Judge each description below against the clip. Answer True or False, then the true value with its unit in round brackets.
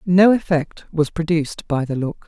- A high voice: False (165 Hz)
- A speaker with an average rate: True (185 wpm)